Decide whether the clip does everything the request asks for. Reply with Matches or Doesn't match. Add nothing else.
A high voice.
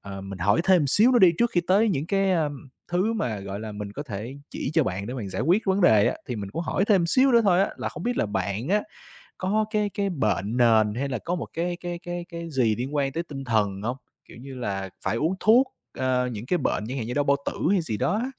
Doesn't match